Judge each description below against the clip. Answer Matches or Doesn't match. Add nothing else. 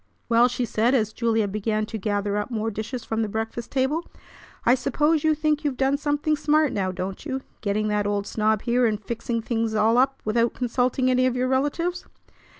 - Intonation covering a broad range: Doesn't match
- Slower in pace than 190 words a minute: Doesn't match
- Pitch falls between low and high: Doesn't match